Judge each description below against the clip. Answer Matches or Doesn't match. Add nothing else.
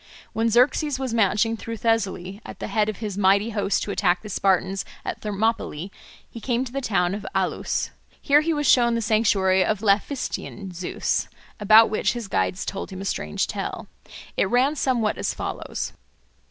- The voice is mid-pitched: Doesn't match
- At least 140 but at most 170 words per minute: Doesn't match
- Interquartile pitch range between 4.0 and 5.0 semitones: Doesn't match